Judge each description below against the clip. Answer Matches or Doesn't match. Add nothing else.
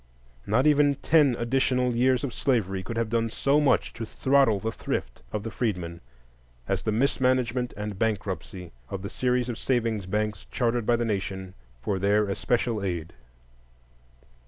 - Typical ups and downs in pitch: Matches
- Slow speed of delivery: Doesn't match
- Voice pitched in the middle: Doesn't match